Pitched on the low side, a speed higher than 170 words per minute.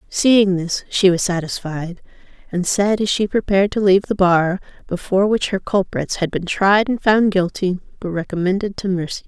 No: high, 190 Hz; average, 180 wpm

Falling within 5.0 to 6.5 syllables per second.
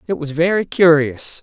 No: 4.7 syllables/s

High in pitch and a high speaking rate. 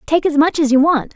Yes: very high, 300 Hz; fast, 310 wpm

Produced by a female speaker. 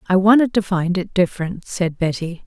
Yes: female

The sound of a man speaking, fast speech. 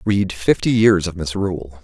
No: male; average, 165 wpm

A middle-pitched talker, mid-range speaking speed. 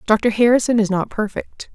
No: high, 220 Hz; average, 170 wpm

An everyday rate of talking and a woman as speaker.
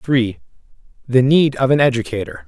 No: average, 145 wpm; male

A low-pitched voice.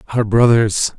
Yes: low, 110 Hz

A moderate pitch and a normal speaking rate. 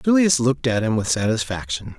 No: low, 125 Hz; average, 180 wpm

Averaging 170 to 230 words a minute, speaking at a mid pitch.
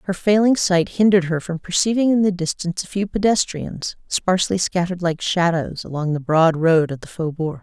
Yes: average, 190 wpm; medium, 175 Hz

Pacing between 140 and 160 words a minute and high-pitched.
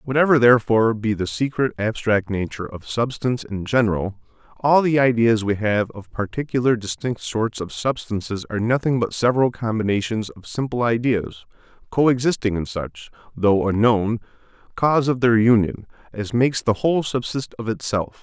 No: average, 155 wpm; low, 115 Hz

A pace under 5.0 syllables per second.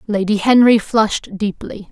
Yes: 4.7 syllables/s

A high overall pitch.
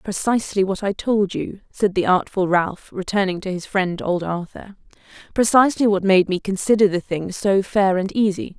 Yes: high, 195 Hz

